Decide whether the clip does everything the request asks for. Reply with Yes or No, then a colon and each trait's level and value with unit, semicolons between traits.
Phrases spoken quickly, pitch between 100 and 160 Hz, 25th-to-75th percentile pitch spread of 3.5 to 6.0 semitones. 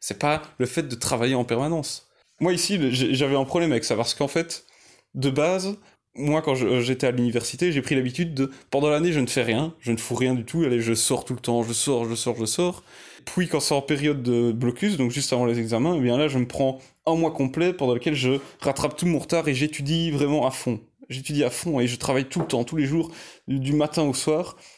Yes: fast, 250 wpm; medium, 140 Hz; average, 4.1 semitones